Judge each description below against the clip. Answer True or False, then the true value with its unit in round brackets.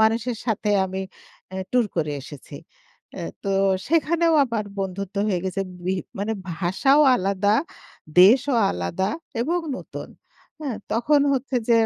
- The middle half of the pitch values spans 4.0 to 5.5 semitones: True (5.2 semitones)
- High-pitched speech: True (210 Hz)